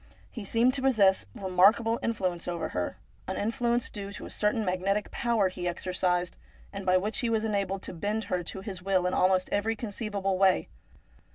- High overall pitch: Yes, high, 195 Hz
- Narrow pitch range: No, average, 3.2 semitones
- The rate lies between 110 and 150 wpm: No, average, 185 wpm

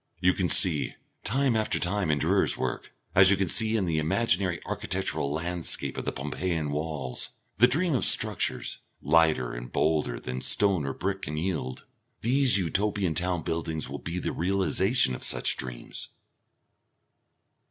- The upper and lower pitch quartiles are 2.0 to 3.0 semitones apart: No, average, 4.6 semitones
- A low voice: Yes, very low, 85 Hz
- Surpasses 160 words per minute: No, average, 155 wpm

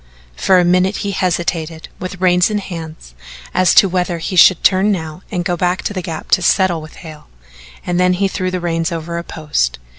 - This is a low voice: No, medium, 180 Hz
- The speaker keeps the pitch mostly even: Yes, narrow, 2.0 semitones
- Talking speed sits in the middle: No, fast, 210 wpm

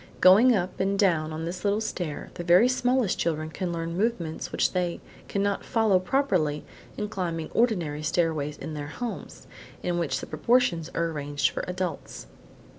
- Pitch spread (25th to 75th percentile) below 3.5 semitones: No, average, 4.3 semitones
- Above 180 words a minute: No, average, 165 wpm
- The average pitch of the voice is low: No, medium, 175 Hz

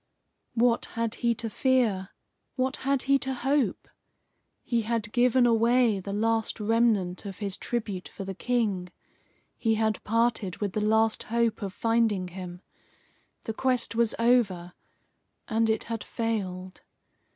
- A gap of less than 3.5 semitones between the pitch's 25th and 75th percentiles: Yes, average, 3.0 semitones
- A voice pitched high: Yes, high, 225 Hz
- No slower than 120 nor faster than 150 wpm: Yes, average, 140 wpm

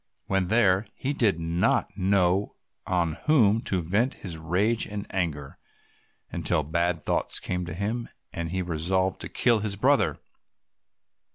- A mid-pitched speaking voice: No, very low, 95 Hz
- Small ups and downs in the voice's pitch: No, average, 3.4 semitones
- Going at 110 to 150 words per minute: Yes, average, 145 wpm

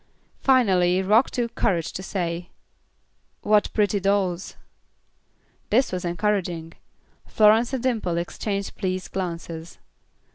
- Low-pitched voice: No, high, 195 Hz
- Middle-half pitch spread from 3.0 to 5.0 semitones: Yes, average, 3.3 semitones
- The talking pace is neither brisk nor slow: No, slow, 105 wpm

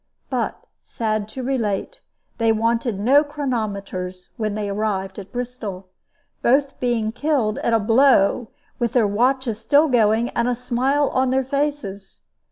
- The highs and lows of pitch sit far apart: No, average, 3.7 semitones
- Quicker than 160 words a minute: No, average, 145 wpm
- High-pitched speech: Yes, high, 230 Hz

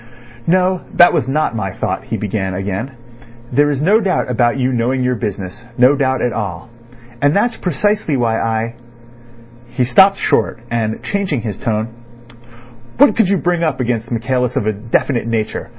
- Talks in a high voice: No, low, 125 Hz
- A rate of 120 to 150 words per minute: No, average, 165 wpm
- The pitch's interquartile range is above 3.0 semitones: Yes, average, 5.2 semitones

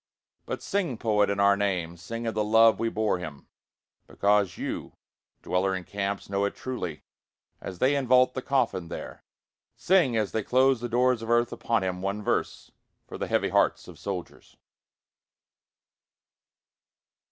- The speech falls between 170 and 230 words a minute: No, average, 155 wpm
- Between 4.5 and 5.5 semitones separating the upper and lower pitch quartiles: No, average, 3.8 semitones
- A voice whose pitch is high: No, low, 105 Hz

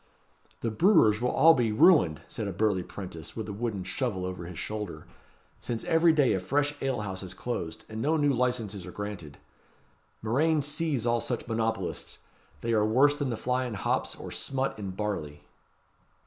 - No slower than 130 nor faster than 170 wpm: No, average, 180 wpm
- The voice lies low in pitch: Yes, low, 110 Hz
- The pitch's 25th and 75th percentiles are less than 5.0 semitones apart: No, wide, 5.6 semitones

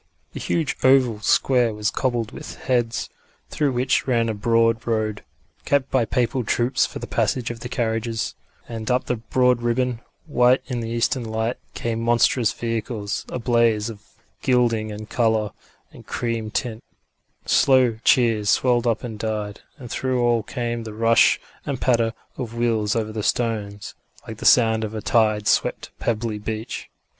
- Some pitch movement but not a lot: No, narrow, 1.9 semitones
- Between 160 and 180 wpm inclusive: Yes, average, 165 wpm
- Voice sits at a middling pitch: No, low, 115 Hz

